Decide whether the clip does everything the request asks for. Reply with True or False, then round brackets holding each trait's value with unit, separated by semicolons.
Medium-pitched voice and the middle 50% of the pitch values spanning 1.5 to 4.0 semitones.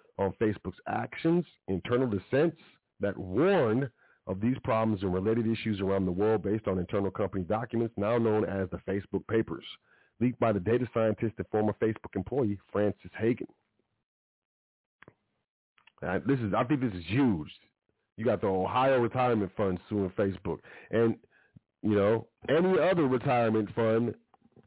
False (110 Hz; 3.0 semitones)